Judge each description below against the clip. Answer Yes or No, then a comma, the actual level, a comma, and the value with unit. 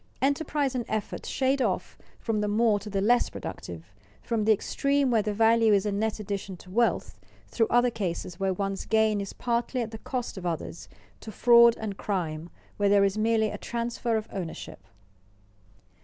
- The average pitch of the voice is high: Yes, high, 220 Hz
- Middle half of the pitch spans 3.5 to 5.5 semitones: No, average, 3.0 semitones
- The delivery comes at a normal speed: Yes, average, 185 wpm